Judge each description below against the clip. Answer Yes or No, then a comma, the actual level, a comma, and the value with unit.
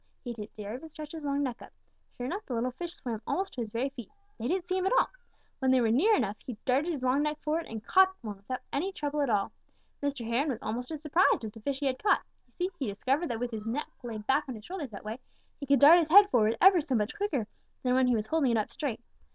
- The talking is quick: Yes, fast, 280 wpm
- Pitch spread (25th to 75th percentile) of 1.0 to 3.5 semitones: No, average, 5.2 semitones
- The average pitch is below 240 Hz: No, very high, 265 Hz